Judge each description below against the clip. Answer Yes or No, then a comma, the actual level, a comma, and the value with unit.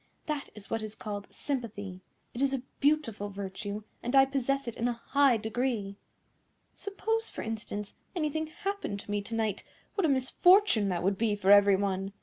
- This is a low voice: No, high, 225 Hz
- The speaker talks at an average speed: Yes, average, 180 wpm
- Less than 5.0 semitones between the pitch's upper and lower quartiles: No, wide, 5.4 semitones